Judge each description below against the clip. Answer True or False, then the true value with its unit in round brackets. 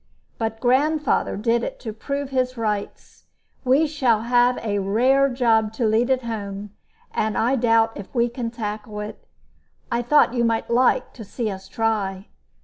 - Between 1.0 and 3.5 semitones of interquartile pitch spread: True (2.8 semitones)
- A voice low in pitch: False (230 Hz)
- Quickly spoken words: False (165 wpm)